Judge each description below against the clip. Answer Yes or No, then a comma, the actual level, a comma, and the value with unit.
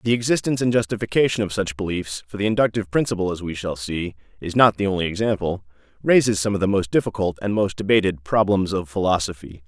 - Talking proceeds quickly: No, average, 185 wpm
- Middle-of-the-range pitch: No, low, 100 Hz